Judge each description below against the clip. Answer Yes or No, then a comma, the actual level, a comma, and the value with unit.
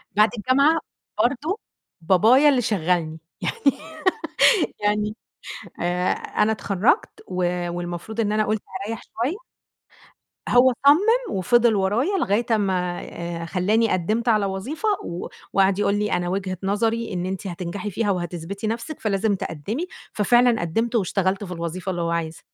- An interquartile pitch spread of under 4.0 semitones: No, average, 4.4 semitones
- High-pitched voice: Yes, high, 205 Hz